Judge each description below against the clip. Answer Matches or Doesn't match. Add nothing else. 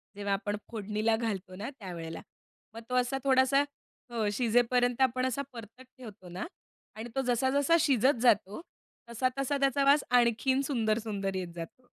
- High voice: Matches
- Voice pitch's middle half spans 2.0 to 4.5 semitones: Matches